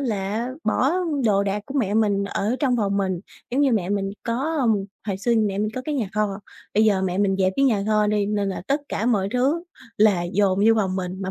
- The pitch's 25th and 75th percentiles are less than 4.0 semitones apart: Yes, average, 3.1 semitones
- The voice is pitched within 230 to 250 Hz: No, high, 210 Hz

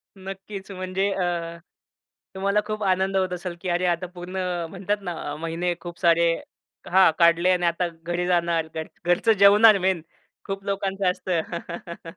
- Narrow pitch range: Yes, narrow, 2.1 semitones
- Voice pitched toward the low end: No, medium, 180 Hz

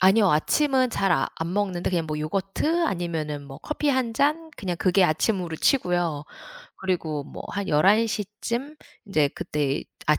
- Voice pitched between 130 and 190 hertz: Yes, medium, 185 Hz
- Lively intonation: Yes, wide, 6.5 semitones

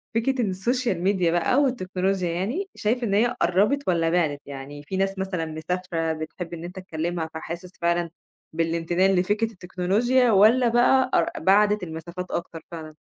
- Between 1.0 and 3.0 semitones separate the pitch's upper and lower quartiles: No, average, 4.0 semitones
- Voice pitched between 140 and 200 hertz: Yes, medium, 185 Hz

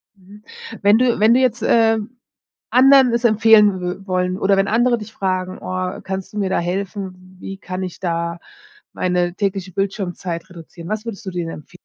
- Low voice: No, high, 195 Hz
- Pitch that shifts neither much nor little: Yes, average, 3.0 semitones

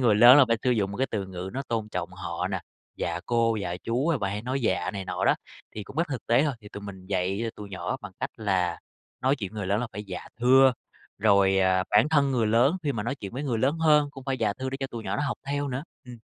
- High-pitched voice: No, low, 115 Hz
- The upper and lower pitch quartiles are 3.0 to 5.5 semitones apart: Yes, average, 5.0 semitones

